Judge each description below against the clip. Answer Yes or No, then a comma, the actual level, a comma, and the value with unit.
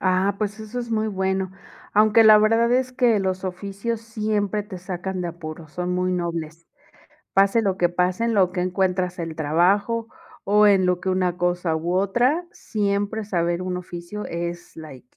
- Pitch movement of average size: Yes, average, 3.1 semitones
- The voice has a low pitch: No, high, 190 Hz